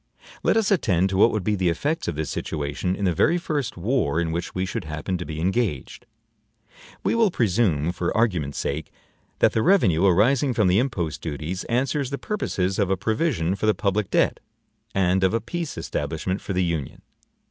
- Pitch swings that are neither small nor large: No, wide, 6.1 semitones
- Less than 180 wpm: No, average, 195 wpm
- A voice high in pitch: No, very low, 95 Hz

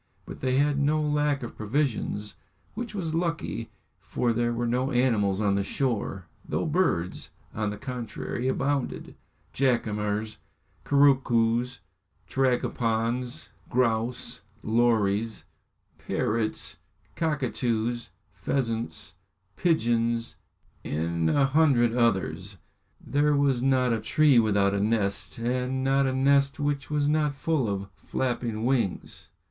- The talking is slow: Yes, slow, 115 wpm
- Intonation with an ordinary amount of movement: Yes, average, 3.9 semitones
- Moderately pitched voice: No, low, 120 Hz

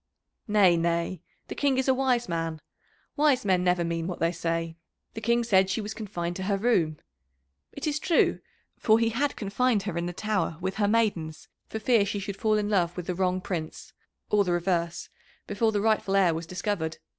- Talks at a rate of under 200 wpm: No, fast, 205 wpm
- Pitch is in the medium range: No, high, 195 Hz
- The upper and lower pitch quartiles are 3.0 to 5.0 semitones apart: Yes, average, 4.2 semitones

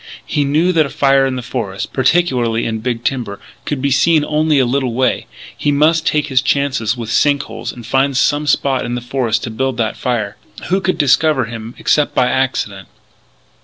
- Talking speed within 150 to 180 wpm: No, average, 200 wpm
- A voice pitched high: No, low, 130 Hz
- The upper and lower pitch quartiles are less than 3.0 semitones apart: No, average, 3.4 semitones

